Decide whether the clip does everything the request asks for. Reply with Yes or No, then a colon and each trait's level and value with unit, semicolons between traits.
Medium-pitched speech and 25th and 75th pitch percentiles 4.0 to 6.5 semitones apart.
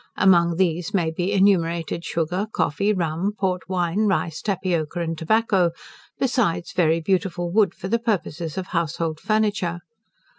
No: medium, 175 Hz; average, 2.9 semitones